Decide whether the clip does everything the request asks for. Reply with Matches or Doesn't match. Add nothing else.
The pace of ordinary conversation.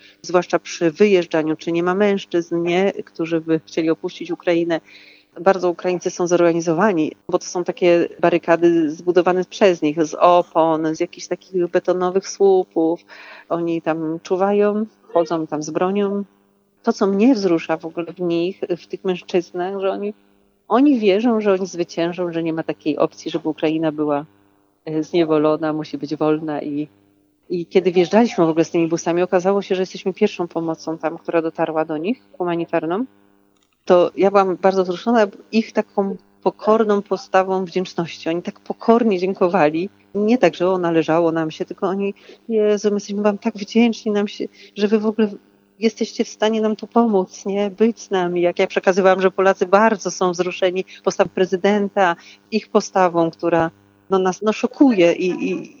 Doesn't match